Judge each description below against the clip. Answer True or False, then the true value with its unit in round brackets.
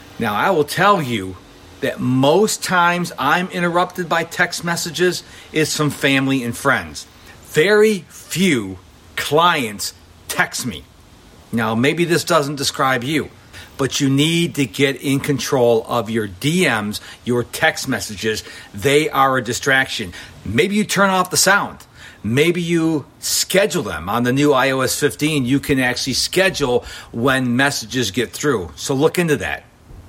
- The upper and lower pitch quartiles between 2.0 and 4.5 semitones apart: False (5.5 semitones)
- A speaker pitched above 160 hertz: False (140 Hz)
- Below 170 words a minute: True (145 wpm)